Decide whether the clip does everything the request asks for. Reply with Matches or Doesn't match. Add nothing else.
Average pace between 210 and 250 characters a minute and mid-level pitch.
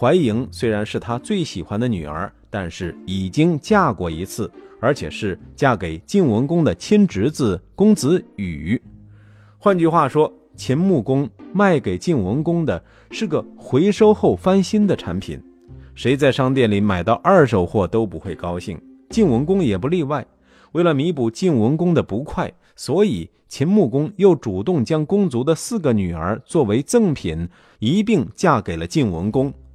Doesn't match